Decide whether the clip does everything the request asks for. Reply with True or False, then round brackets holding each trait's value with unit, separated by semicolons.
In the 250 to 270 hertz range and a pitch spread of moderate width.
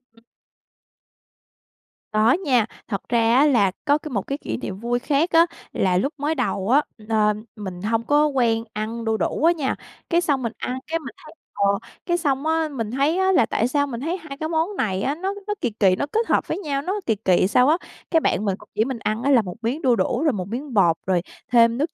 False (255 Hz; 5.8 semitones)